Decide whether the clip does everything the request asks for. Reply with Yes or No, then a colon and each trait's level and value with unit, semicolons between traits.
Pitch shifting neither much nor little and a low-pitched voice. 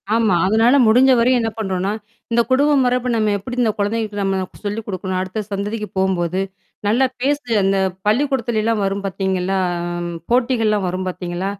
No: average, 3.7 semitones; high, 210 Hz